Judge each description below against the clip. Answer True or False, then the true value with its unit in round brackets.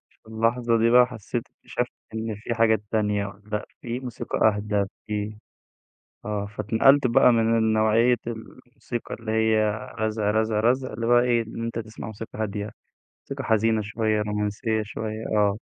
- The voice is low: True (110 Hz)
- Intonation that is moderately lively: False (1.6 semitones)